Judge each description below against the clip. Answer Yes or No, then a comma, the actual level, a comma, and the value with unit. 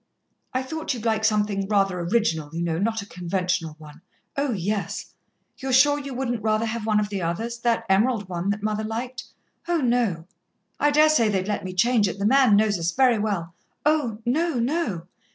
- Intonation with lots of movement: No, average, 4.4 semitones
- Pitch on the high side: Yes, high, 215 Hz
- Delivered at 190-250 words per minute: Yes, average, 195 wpm